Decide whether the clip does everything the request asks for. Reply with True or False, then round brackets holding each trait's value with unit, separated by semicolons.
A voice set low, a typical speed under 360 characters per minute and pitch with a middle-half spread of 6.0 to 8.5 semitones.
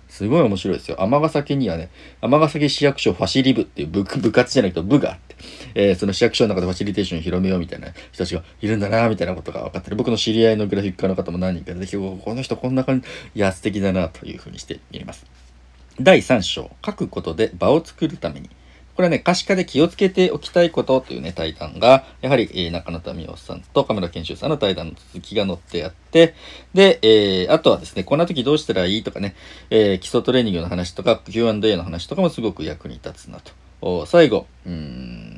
False (100 Hz; 455 characters per minute; 6.8 semitones)